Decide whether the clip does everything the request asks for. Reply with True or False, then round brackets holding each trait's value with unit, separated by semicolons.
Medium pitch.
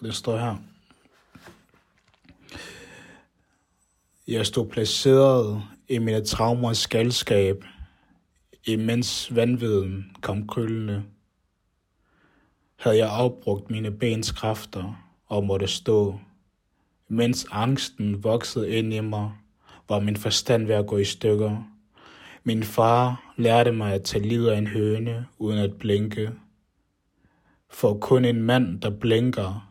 False (110 Hz)